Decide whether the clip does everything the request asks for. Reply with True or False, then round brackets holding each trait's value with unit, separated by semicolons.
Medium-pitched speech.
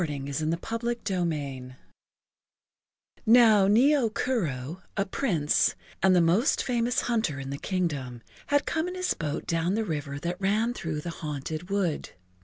True (180 Hz)